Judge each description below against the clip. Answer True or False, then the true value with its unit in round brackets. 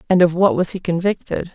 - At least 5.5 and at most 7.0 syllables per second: True (5.8 syllables/s)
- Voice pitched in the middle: True (175 Hz)